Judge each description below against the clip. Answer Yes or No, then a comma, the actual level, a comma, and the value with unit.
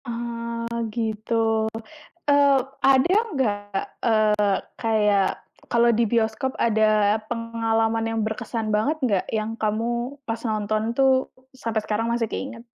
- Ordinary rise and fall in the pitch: No, narrow, 1.6 semitones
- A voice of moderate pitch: No, high, 230 Hz